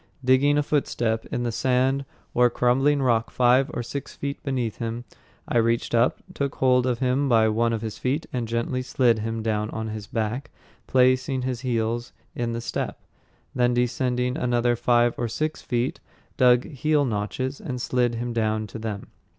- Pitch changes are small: Yes, narrow, 2.0 semitones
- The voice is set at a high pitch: No, low, 120 Hz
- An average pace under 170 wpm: No, average, 175 wpm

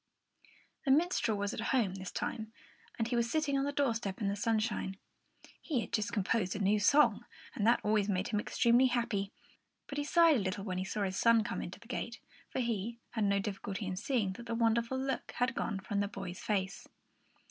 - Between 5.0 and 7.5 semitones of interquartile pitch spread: No, average, 3.3 semitones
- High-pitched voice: Yes, high, 220 Hz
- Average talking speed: No, fast, 220 wpm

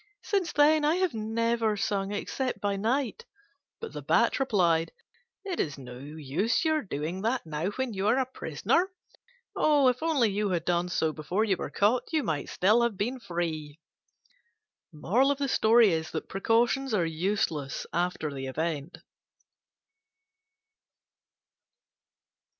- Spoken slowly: Yes, slow, 125 wpm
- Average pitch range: No, wide, 7.7 semitones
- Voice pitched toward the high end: Yes, high, 205 Hz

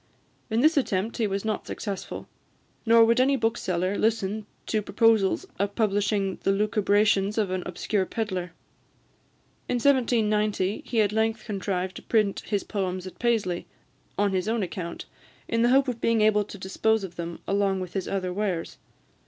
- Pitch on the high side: Yes, high, 205 Hz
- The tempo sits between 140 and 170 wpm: Yes, average, 165 wpm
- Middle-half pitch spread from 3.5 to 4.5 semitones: No, average, 2.8 semitones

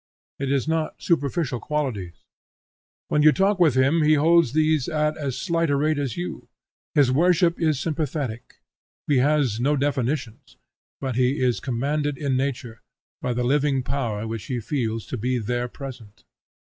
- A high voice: No, medium, 140 Hz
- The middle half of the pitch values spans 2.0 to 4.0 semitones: Yes, average, 3.6 semitones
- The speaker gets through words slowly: No, average, 160 wpm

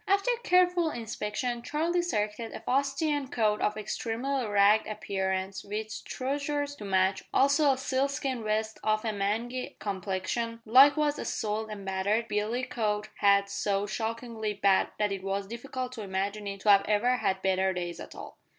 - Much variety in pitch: No, average, 4.3 semitones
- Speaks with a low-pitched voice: No, high, 215 Hz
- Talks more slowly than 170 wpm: Yes, average, 160 wpm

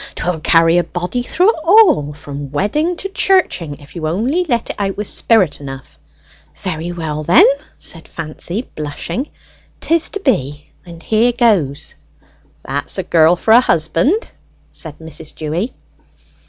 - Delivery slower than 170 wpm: Yes, average, 150 wpm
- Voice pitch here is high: No, medium, 175 Hz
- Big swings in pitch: Yes, wide, 7.7 semitones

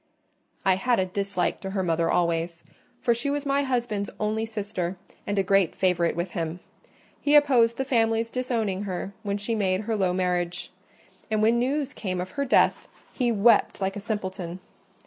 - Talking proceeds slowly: No, average, 180 wpm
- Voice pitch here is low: No, high, 205 Hz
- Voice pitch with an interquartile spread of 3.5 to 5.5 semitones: Yes, average, 4.1 semitones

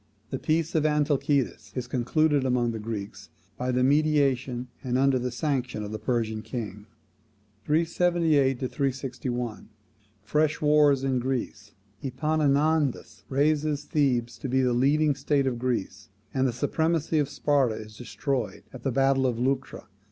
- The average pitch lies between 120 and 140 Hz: Yes, low, 135 Hz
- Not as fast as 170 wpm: Yes, average, 145 wpm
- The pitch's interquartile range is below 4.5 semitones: Yes, average, 3.3 semitones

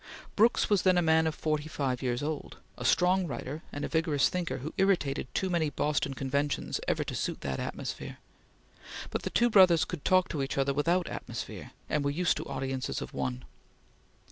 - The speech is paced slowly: No, average, 195 wpm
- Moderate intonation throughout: Yes, average, 4.5 semitones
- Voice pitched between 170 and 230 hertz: No, medium, 150 Hz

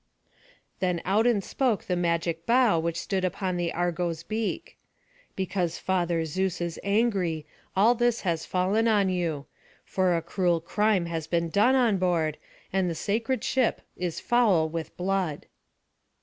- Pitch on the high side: No, medium, 180 Hz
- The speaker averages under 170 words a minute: Yes, average, 150 wpm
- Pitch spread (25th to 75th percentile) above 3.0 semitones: Yes, average, 3.7 semitones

